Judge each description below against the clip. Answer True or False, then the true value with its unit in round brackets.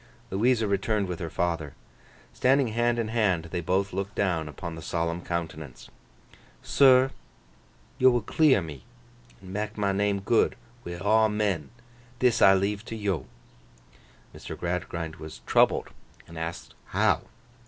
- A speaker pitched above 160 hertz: False (100 Hz)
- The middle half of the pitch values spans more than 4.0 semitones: True (4.6 semitones)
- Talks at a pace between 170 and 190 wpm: False (145 wpm)